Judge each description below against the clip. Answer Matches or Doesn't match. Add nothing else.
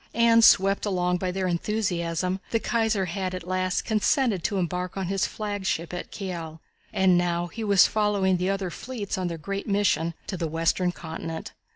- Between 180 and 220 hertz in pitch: Matches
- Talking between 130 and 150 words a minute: Doesn't match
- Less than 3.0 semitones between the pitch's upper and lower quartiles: Matches